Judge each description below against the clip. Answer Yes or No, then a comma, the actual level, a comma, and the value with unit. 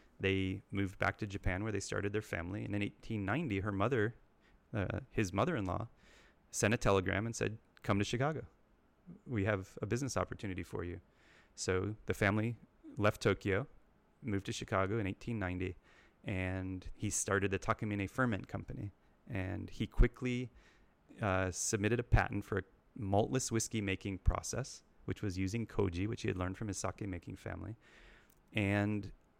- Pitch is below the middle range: Yes, low, 100 Hz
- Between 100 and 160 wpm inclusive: Yes, average, 155 wpm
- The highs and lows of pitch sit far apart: No, average, 2.9 semitones